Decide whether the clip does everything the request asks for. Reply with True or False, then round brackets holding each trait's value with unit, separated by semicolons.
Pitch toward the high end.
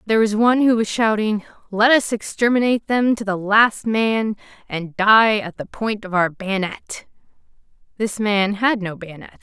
True (215 Hz)